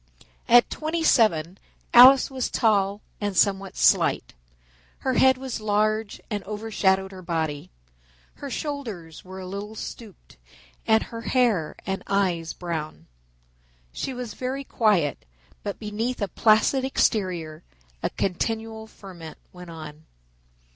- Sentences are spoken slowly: Yes, slow, 125 wpm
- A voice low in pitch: No, high, 205 Hz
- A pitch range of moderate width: Yes, average, 4.4 semitones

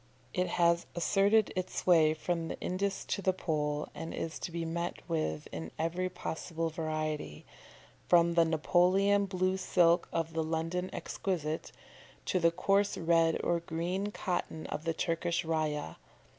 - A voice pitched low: No, medium, 170 Hz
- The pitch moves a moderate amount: No, narrow, 2.2 semitones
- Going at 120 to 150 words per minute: Yes, average, 145 wpm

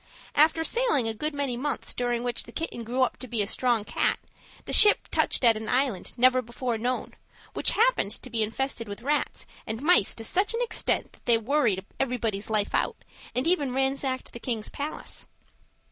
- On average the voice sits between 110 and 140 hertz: No, very high, 250 Hz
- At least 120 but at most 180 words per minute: No, average, 190 wpm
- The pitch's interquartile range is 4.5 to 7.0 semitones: No, average, 4.1 semitones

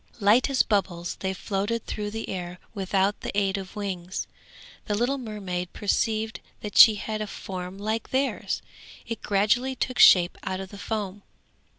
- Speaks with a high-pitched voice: Yes, high, 205 Hz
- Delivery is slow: No, average, 165 wpm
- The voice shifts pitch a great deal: No, narrow, 2.5 semitones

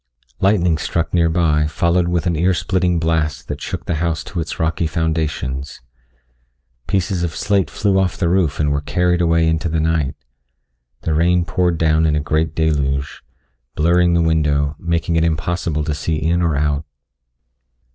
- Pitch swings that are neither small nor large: No, narrow, 2.1 semitones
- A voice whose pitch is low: Yes, very low, 80 Hz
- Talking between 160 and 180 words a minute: Yes, average, 170 wpm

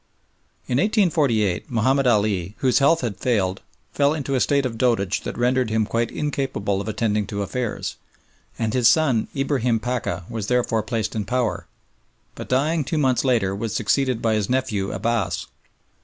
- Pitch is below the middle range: Yes, low, 120 Hz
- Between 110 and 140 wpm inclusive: No, average, 165 wpm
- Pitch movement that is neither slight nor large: Yes, average, 3.7 semitones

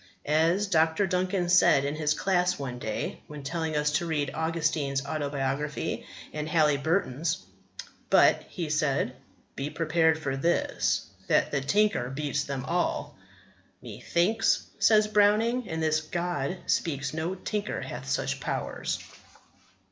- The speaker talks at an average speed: No, slow, 130 wpm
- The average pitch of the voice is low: No, medium, 160 Hz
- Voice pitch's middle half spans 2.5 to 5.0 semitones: Yes, average, 3.7 semitones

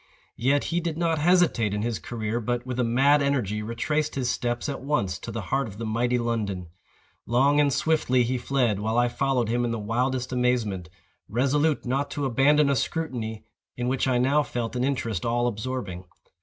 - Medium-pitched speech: No, low, 125 Hz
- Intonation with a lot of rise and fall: No, average, 3.3 semitones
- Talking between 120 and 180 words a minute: No, average, 195 wpm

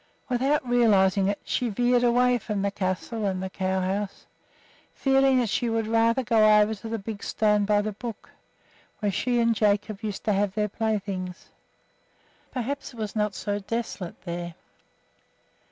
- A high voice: Yes, high, 215 Hz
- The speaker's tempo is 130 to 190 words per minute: Yes, average, 165 wpm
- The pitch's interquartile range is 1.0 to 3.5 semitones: Yes, average, 3.0 semitones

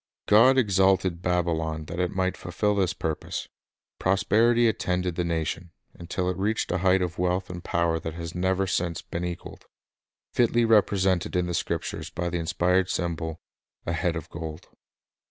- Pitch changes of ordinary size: No, narrow, 2.1 semitones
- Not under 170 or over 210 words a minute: Yes, average, 175 wpm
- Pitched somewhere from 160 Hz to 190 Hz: No, very low, 90 Hz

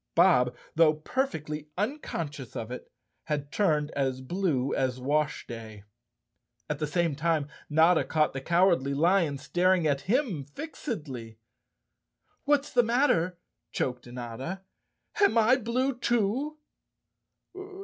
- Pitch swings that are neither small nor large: No, wide, 6.7 semitones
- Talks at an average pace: No, slow, 115 wpm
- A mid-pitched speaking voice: Yes, medium, 155 Hz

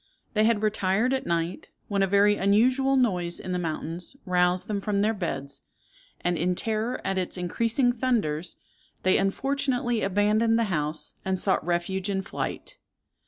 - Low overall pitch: No, high, 195 Hz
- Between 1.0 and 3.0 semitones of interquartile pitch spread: No, average, 4.1 semitones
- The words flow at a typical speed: Yes, average, 160 wpm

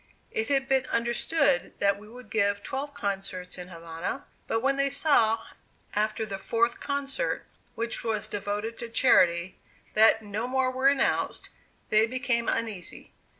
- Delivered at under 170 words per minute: Yes, average, 150 wpm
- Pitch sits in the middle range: No, high, 225 Hz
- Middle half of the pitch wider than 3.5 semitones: Yes, average, 4.5 semitones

